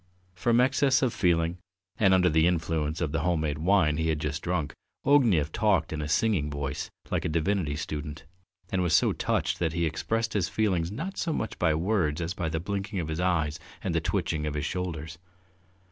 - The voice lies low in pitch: Yes, very low, 85 Hz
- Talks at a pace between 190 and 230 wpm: Yes, fast, 205 wpm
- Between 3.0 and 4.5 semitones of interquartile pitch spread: Yes, average, 4.1 semitones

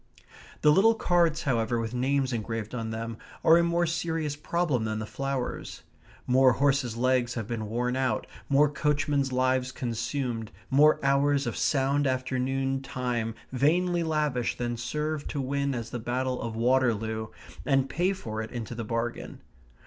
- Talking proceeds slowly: No, average, 155 wpm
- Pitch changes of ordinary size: Yes, average, 3.5 semitones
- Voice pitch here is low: Yes, low, 130 Hz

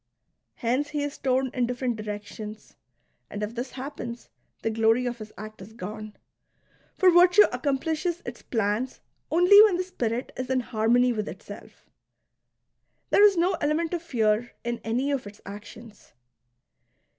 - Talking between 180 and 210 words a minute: No, average, 150 wpm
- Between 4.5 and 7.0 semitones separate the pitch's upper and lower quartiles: Yes, average, 5.1 semitones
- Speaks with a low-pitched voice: No, high, 245 Hz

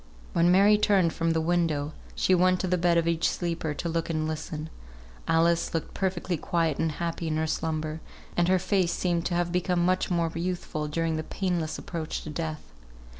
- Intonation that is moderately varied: No, narrow, 1.9 semitones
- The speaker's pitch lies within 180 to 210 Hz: No, medium, 170 Hz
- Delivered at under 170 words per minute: No, average, 195 wpm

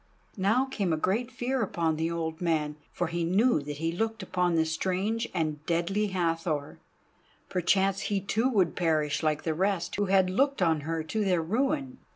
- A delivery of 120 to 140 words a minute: No, average, 185 wpm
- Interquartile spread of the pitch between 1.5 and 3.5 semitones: No, average, 4.3 semitones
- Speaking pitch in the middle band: Yes, medium, 180 Hz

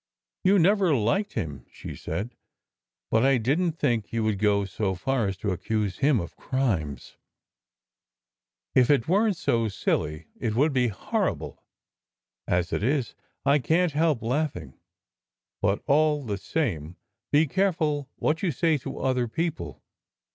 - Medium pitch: No, low, 125 Hz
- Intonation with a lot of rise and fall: Yes, wide, 7.1 semitones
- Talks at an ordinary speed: Yes, average, 155 wpm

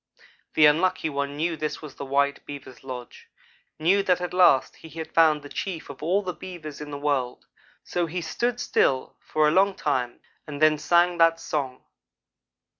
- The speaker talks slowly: No, average, 185 wpm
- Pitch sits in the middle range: Yes, medium, 155 Hz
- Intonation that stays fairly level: No, average, 3.6 semitones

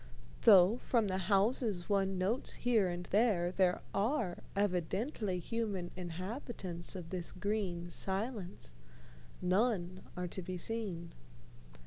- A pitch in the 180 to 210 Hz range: Yes, high, 190 Hz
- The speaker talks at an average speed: No, slow, 115 wpm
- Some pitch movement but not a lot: Yes, average, 3.5 semitones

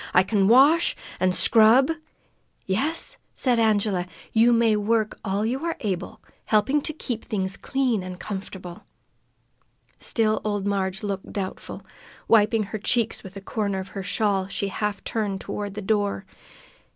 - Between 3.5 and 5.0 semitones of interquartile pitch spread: No, average, 2.8 semitones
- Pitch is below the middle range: No, high, 210 Hz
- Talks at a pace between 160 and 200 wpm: No, average, 150 wpm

